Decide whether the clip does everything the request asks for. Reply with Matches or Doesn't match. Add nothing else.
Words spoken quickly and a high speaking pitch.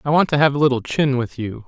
Doesn't match